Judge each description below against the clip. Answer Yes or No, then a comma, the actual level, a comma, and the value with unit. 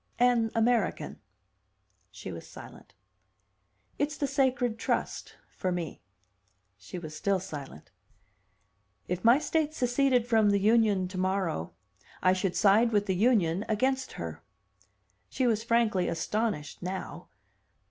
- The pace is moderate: No, slow, 120 wpm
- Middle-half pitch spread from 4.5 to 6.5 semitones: Yes, average, 4.9 semitones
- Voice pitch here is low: No, high, 210 Hz